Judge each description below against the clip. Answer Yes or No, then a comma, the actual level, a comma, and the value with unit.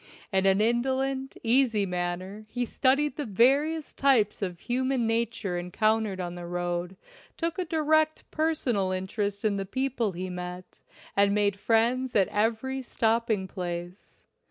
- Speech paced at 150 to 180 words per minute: No, average, 140 wpm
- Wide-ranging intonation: Yes, wide, 5.7 semitones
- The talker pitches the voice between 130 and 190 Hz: No, high, 220 Hz